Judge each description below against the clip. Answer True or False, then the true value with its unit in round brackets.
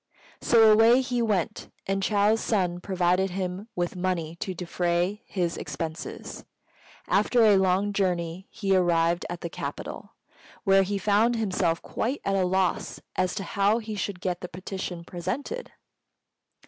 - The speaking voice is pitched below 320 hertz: True (190 Hz)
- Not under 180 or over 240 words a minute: False (150 wpm)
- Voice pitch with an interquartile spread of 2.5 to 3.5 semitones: True (2.9 semitones)